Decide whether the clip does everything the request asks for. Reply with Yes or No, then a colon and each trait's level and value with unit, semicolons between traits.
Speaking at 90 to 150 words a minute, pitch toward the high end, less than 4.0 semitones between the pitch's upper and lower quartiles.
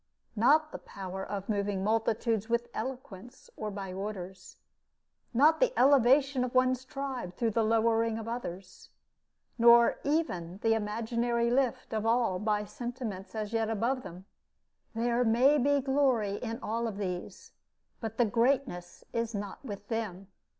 Yes: average, 145 wpm; high, 230 Hz; average, 3.5 semitones